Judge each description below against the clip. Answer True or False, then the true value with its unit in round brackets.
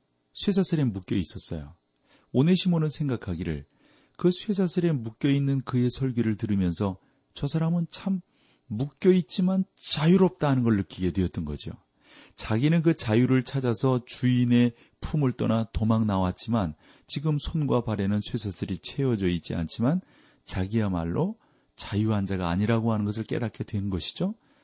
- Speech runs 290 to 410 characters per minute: True (315 characters per minute)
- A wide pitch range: True (7.5 semitones)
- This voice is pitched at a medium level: False (120 Hz)